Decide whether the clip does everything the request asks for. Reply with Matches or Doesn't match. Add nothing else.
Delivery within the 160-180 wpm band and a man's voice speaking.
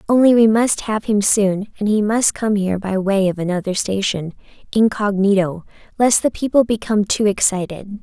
Doesn't match